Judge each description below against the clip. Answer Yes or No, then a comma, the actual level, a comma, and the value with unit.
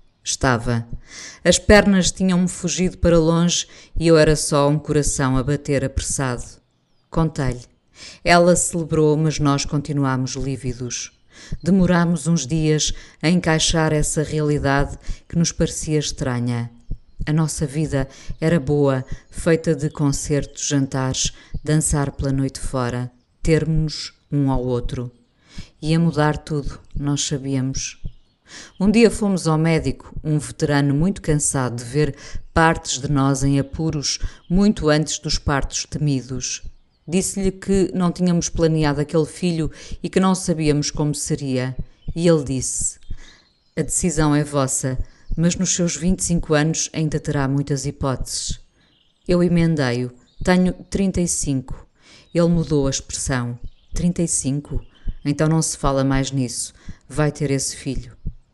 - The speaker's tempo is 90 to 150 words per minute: Yes, average, 130 wpm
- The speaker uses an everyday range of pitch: Yes, average, 3.5 semitones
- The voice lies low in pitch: No, medium, 150 Hz